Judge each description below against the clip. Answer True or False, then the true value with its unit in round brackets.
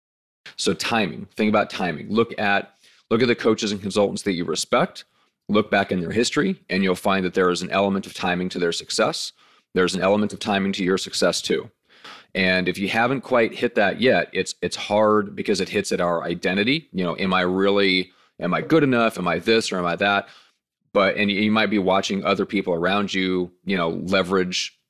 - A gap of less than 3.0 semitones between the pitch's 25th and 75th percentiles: True (2.4 semitones)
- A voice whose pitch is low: True (100 Hz)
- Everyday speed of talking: False (215 wpm)